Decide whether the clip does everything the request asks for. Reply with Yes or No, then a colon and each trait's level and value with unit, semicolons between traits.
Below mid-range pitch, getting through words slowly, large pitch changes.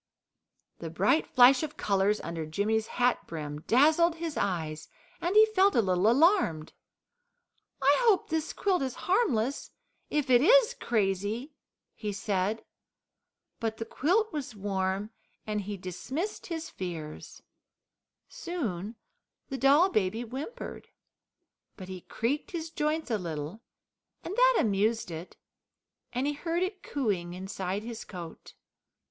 No: high, 230 Hz; slow, 130 wpm; wide, 8.7 semitones